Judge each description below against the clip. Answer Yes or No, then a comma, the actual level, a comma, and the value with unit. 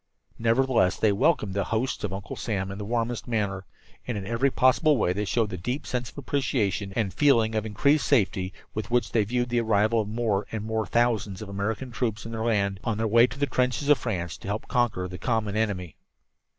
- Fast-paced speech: Yes, fast, 215 wpm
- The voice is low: Yes, low, 110 Hz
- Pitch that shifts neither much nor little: Yes, average, 3.4 semitones